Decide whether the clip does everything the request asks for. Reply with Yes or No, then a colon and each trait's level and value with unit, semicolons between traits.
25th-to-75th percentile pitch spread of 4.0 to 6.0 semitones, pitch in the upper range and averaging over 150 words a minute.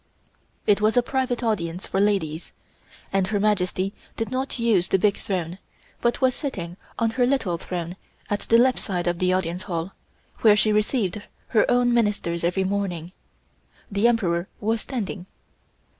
Yes: average, 4.3 semitones; high, 200 Hz; average, 160 wpm